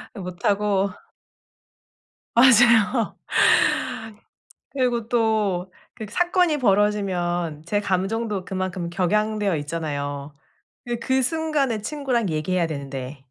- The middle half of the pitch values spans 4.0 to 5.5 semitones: Yes, average, 5.1 semitones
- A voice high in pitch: Yes, high, 205 Hz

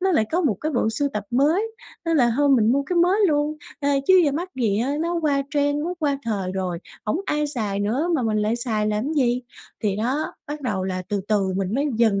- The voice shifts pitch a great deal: Yes, wide, 6.0 semitones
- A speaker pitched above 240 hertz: Yes, very high, 255 Hz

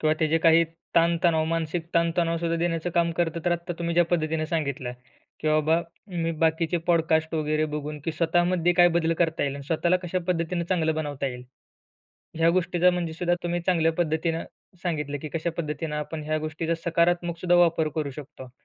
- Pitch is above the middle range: No, medium, 165 Hz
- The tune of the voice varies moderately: No, narrow, 1.8 semitones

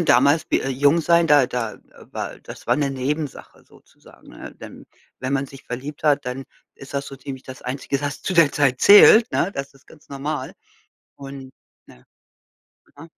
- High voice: No, medium, 140 Hz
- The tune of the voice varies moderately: No, narrow, 2.0 semitones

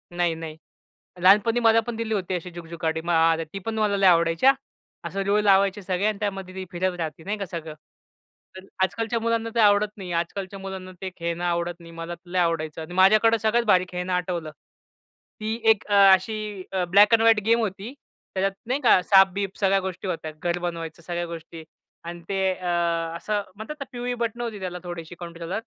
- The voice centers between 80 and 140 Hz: No, high, 190 Hz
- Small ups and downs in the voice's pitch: No, average, 3.5 semitones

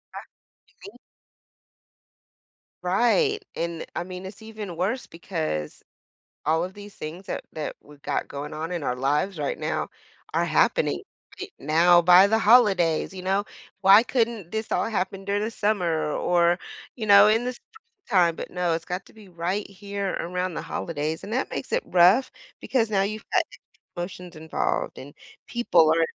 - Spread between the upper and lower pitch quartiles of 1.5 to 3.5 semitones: No, average, 4.2 semitones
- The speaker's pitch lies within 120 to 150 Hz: No, medium, 185 Hz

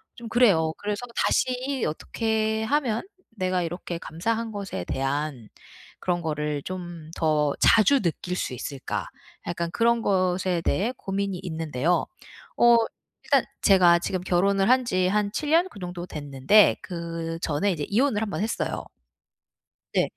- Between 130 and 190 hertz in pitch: Yes, medium, 185 Hz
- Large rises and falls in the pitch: No, average, 4.9 semitones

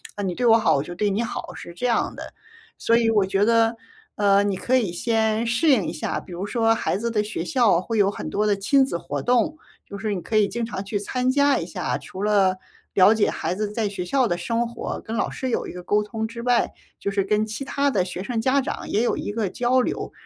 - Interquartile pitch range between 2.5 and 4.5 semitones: Yes, average, 3.1 semitones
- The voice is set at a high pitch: Yes, high, 215 Hz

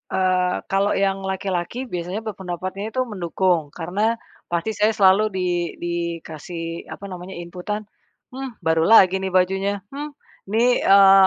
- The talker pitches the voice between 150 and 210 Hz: Yes, high, 190 Hz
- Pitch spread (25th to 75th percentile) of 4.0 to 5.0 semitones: No, average, 2.7 semitones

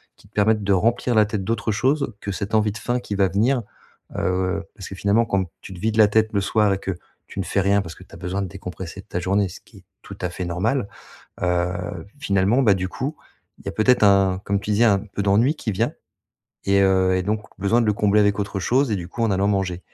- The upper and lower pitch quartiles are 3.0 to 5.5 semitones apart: No, narrow, 2.4 semitones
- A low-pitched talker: Yes, low, 100 Hz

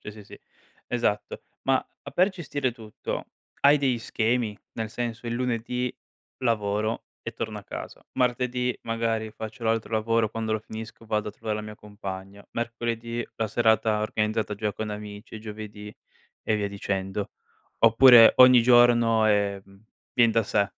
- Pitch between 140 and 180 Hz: No, low, 110 Hz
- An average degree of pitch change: No, narrow, 2.1 semitones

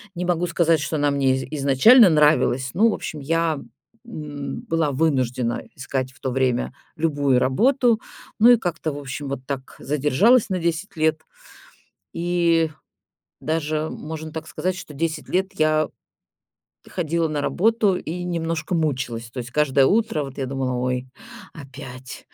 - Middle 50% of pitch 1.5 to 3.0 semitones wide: No, average, 4.0 semitones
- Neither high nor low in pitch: Yes, medium, 155 Hz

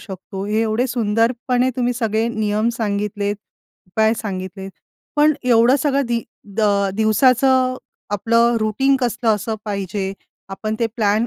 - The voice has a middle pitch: No, high, 225 Hz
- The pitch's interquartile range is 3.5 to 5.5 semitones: No, average, 2.9 semitones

